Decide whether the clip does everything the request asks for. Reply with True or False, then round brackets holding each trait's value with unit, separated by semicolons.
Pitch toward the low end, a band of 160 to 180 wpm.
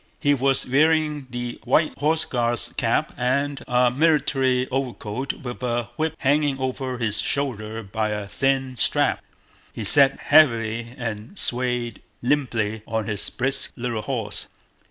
False (125 Hz; 135 wpm)